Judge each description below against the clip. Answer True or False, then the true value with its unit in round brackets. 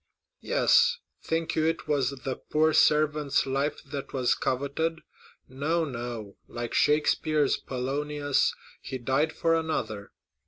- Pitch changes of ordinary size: True (3.2 semitones)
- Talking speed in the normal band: False (115 wpm)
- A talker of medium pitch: True (145 Hz)